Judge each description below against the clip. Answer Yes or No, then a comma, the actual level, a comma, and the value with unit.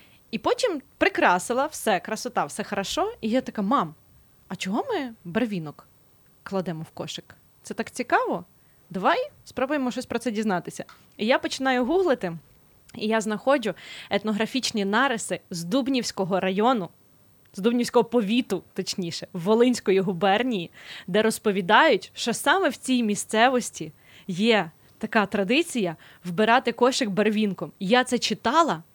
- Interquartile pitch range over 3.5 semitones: Yes, average, 5.0 semitones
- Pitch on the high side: Yes, high, 220 Hz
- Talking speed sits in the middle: Yes, average, 125 wpm